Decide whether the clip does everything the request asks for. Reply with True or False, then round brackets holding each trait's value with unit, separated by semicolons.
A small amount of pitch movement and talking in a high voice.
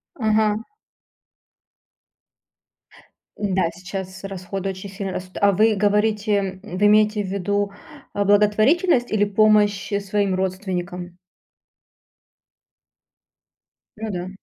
True (1.9 semitones; 200 Hz)